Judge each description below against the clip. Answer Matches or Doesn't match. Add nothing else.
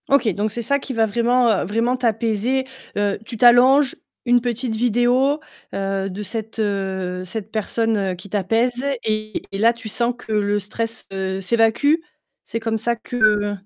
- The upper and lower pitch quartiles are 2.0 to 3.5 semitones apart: Matches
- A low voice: Doesn't match